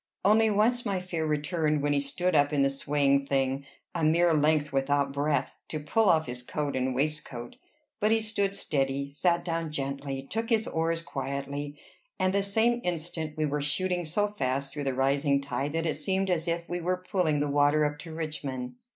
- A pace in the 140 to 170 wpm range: No, average, 195 wpm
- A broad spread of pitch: No, average, 4.0 semitones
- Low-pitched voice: No, medium, 150 Hz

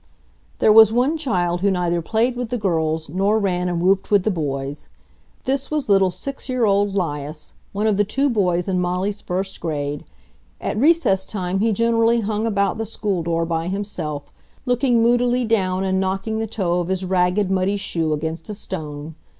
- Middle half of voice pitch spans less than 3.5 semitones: No, average, 4.1 semitones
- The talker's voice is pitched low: No, high, 195 Hz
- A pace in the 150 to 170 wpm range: No, average, 185 wpm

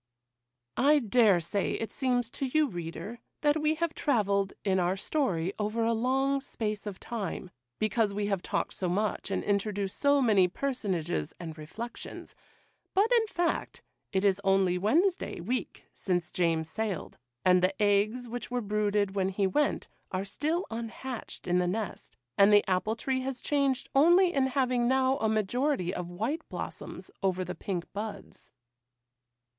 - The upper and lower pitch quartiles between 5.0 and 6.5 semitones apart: Yes, wide, 5.5 semitones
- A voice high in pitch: Yes, high, 215 Hz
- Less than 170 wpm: Yes, average, 160 wpm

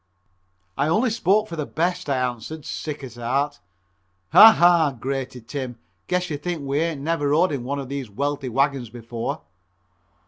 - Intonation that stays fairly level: No, average, 4.2 semitones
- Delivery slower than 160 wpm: No, average, 170 wpm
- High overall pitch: No, medium, 145 Hz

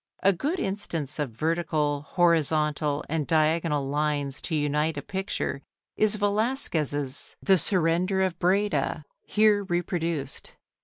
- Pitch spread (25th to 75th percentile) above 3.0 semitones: Yes, average, 4.4 semitones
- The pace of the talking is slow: Yes, slow, 115 wpm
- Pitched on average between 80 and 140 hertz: No, medium, 165 Hz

